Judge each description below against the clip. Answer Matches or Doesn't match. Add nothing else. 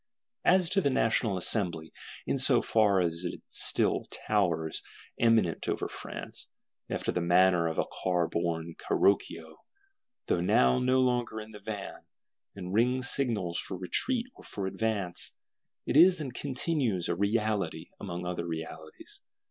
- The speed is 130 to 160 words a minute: Matches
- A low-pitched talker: Matches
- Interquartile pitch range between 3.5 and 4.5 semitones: Doesn't match